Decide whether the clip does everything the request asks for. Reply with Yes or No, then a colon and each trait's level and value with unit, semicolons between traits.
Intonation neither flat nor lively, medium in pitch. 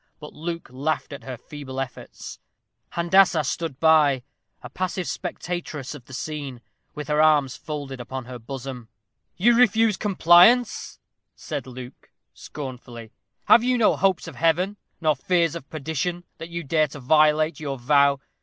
Yes: average, 4.4 semitones; medium, 150 Hz